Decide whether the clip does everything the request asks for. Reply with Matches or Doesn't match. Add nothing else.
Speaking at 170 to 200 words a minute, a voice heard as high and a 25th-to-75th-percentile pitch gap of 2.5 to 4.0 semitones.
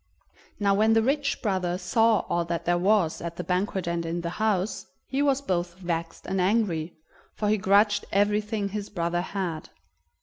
Matches